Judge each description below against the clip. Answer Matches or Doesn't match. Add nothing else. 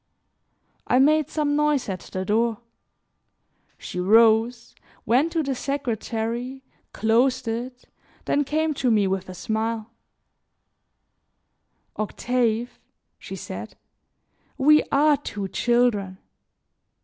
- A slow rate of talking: Matches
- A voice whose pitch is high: Matches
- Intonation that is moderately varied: Matches